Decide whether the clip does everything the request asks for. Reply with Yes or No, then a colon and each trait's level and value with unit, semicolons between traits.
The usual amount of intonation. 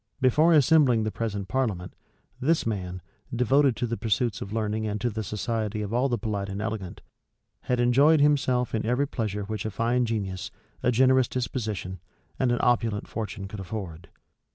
Yes: average, 3.4 semitones